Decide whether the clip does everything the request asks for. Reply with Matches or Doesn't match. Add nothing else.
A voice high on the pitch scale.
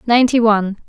Matches